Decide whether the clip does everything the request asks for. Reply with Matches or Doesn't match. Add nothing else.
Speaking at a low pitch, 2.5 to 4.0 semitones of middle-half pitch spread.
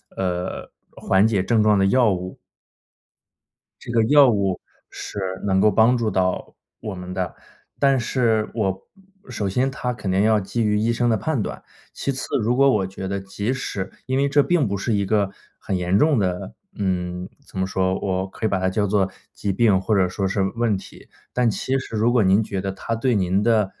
Matches